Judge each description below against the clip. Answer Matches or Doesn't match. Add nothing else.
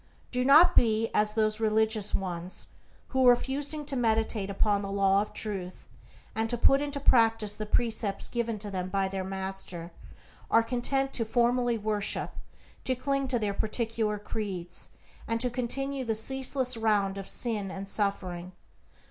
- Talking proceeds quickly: Doesn't match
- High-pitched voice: Matches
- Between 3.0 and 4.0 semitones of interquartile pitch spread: Matches